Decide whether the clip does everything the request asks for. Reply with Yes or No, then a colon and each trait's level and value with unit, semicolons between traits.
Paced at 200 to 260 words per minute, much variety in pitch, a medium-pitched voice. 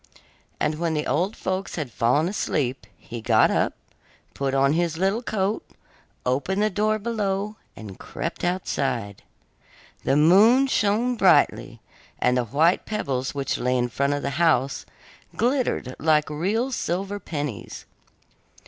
No: average, 140 wpm; wide, 6.9 semitones; medium, 165 Hz